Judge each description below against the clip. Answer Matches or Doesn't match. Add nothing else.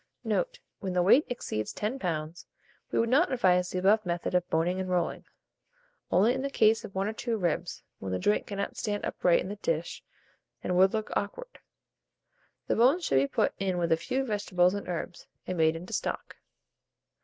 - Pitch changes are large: Doesn't match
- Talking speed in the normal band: Matches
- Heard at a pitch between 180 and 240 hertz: Matches